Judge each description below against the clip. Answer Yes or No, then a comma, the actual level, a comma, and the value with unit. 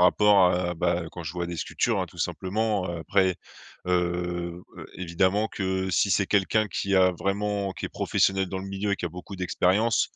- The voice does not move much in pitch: Yes, narrow, 2.0 semitones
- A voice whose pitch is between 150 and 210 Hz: No, very low, 95 Hz